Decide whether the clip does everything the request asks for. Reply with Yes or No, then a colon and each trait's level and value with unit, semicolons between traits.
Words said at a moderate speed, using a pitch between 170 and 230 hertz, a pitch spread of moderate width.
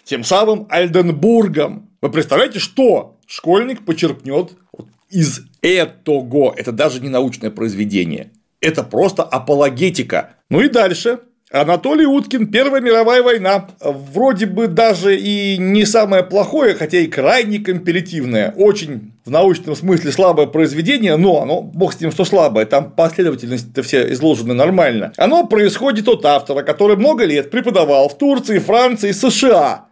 No: average, 135 wpm; medium, 185 Hz; wide, 7.3 semitones